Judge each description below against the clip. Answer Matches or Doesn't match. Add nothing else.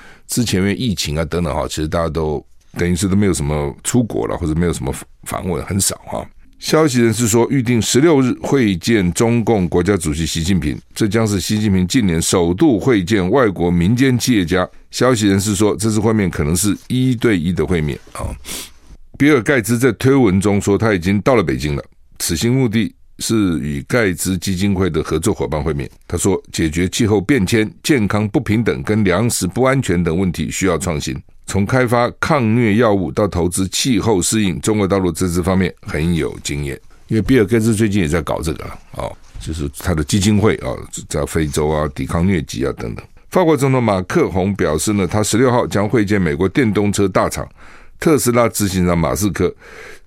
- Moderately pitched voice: Doesn't match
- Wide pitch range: Doesn't match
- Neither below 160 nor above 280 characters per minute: Doesn't match